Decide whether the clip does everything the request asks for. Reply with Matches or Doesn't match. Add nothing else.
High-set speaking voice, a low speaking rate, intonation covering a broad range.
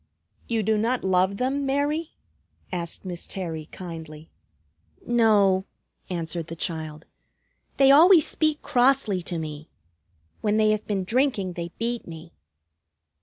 Matches